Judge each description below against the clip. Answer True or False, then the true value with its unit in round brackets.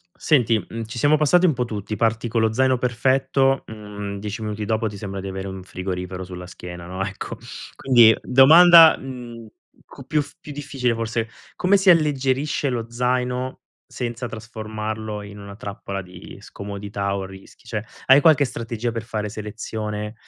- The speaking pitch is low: True (115 Hz)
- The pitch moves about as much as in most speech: True (4.1 semitones)